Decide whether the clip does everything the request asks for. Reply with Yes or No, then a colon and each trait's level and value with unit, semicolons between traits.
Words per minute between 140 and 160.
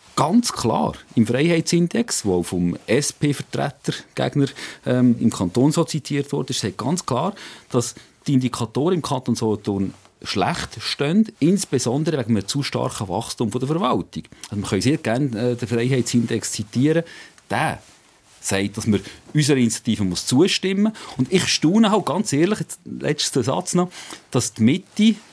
Yes: average, 150 wpm